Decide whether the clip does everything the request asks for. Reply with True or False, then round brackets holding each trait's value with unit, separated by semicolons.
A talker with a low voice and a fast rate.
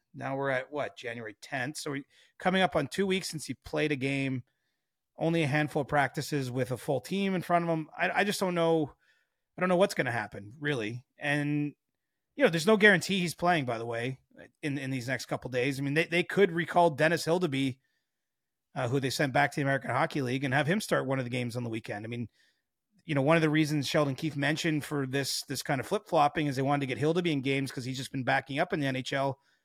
False (145 Hz; 255 wpm)